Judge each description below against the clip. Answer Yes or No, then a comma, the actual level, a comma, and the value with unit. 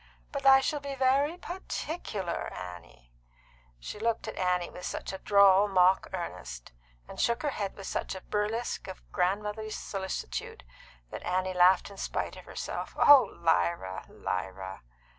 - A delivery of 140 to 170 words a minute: Yes, average, 150 wpm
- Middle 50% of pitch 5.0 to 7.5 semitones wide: Yes, average, 5.3 semitones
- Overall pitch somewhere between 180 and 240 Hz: Yes, high, 190 Hz